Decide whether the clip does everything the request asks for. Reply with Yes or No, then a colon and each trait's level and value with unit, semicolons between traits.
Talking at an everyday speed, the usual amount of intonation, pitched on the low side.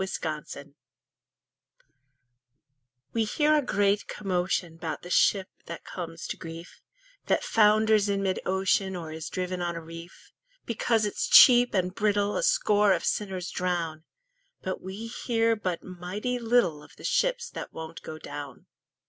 No: average, 150 wpm; average, 4.2 semitones; high, 190 Hz